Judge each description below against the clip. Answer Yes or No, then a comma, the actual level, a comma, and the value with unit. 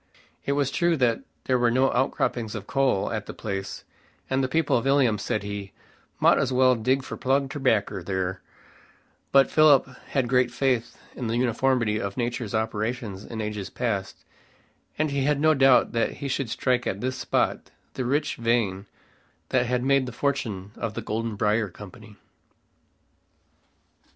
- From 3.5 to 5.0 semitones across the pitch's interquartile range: Yes, average, 3.9 semitones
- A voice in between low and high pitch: No, low, 120 Hz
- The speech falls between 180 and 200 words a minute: No, average, 165 wpm